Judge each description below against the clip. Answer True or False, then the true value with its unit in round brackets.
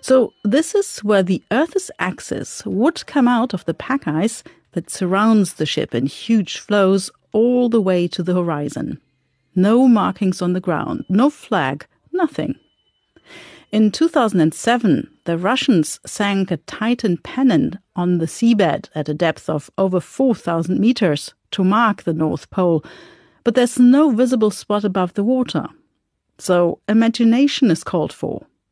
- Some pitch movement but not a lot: False (5.9 semitones)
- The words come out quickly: False (150 wpm)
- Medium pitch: False (210 Hz)